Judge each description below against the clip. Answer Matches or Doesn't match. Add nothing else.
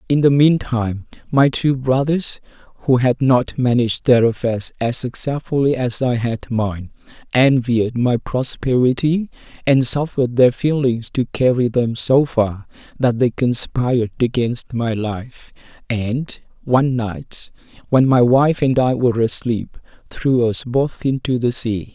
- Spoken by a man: Matches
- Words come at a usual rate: Matches